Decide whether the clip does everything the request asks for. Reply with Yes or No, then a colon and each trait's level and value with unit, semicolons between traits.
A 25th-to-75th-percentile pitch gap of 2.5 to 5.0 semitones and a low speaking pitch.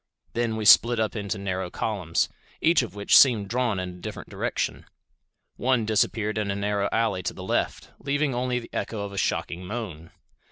Yes: average, 3.2 semitones; low, 105 Hz